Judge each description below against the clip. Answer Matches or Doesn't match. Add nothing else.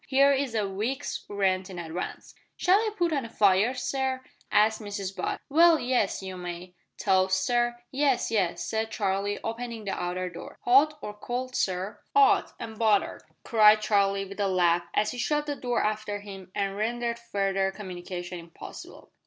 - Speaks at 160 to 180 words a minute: Matches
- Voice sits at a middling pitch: Doesn't match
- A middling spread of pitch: Matches